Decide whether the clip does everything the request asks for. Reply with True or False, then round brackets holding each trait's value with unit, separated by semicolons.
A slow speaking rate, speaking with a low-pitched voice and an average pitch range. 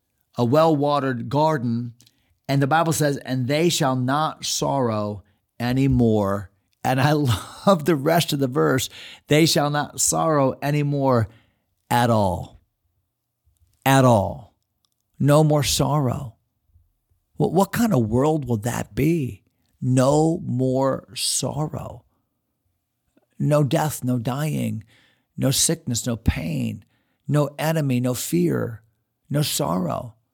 True (115 wpm; 130 Hz; 4.4 semitones)